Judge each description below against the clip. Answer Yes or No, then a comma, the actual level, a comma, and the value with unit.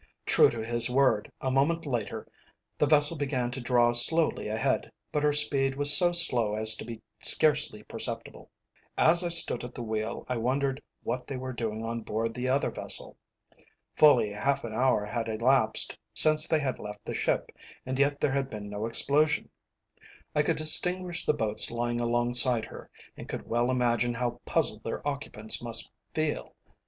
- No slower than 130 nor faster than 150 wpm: No, average, 175 wpm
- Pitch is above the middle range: No, low, 125 Hz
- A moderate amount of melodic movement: Yes, average, 4.0 semitones